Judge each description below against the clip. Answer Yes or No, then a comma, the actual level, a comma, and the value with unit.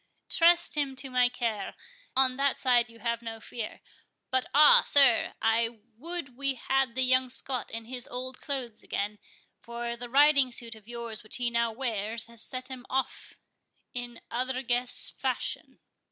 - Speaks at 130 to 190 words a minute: Yes, average, 160 wpm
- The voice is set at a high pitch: Yes, high, 245 Hz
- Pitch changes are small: Yes, narrow, 2.2 semitones